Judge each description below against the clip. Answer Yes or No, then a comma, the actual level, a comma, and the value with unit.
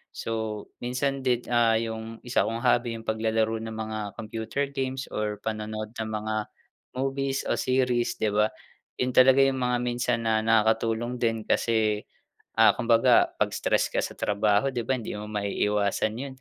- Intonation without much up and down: Yes, narrow, 2.3 semitones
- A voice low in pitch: Yes, low, 115 Hz